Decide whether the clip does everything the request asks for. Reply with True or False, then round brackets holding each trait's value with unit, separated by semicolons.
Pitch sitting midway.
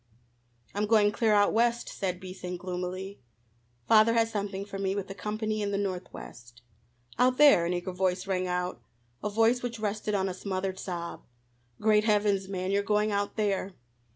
False (200 Hz)